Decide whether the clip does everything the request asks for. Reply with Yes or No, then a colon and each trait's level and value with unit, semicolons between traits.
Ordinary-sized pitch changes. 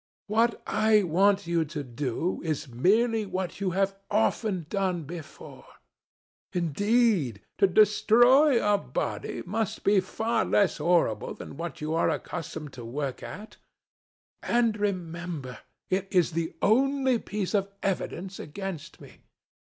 Yes: average, 4.6 semitones